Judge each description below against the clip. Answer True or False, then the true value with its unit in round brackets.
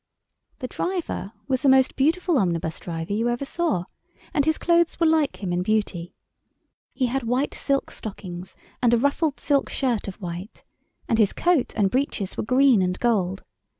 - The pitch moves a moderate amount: False (6.6 semitones)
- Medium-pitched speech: False (240 Hz)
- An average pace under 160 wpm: False (175 wpm)